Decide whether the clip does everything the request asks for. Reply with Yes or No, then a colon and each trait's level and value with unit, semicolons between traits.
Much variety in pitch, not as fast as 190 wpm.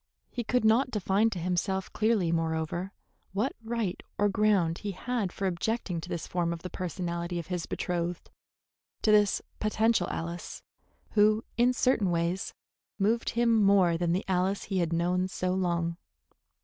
No: average, 3.7 semitones; average, 160 wpm